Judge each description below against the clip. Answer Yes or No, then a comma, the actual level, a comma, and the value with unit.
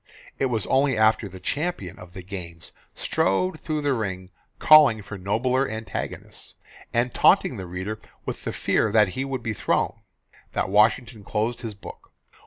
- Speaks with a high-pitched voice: No, low, 110 Hz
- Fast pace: No, average, 165 wpm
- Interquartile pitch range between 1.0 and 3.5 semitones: No, average, 4.9 semitones